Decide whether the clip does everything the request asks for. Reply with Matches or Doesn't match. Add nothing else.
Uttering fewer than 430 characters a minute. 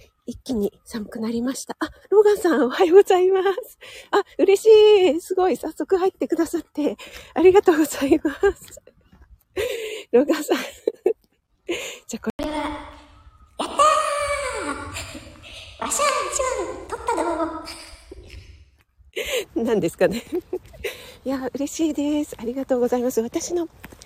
Matches